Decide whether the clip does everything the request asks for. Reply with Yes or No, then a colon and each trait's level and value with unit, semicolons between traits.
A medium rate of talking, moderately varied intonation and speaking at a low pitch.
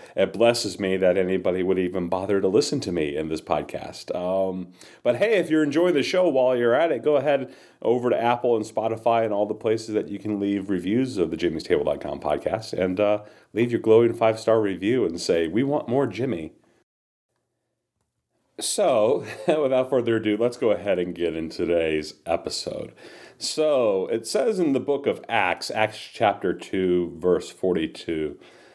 Yes: average, 180 wpm; average, 4.2 semitones; low, 105 Hz